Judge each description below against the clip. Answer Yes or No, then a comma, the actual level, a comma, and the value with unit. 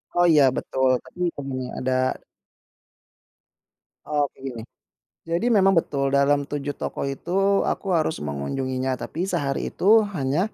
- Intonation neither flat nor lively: Yes, average, 3.7 semitones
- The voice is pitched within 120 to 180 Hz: Yes, medium, 140 Hz